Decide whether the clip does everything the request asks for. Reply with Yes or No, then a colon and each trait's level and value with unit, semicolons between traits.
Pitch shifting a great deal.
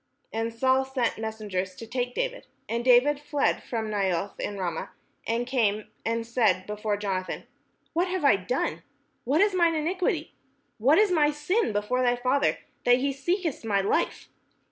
Yes: wide, 5.7 semitones